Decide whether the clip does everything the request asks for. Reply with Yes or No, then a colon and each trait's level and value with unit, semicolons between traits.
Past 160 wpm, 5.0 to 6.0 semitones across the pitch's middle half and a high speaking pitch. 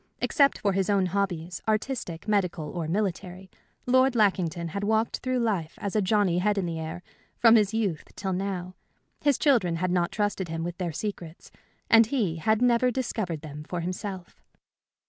No: average, 170 wpm; average, 4.0 semitones; high, 195 Hz